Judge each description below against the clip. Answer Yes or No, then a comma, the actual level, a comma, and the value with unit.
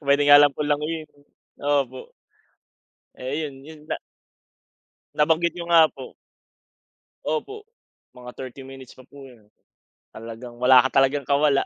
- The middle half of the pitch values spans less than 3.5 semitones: Yes, narrow, 2.6 semitones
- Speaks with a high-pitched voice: No, medium, 140 Hz